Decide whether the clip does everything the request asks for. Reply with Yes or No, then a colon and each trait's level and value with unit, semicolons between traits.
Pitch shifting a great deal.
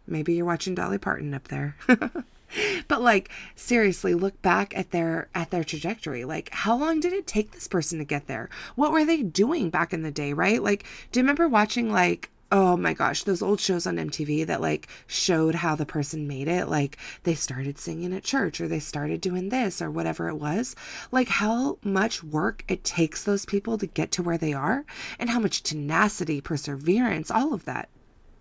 Yes: wide, 5.8 semitones